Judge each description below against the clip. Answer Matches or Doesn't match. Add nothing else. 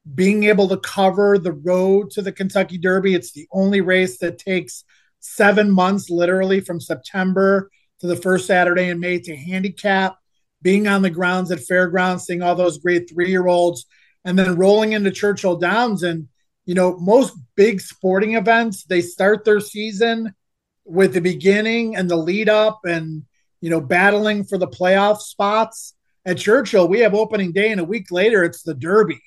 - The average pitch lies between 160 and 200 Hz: Matches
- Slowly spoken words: Doesn't match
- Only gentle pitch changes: Matches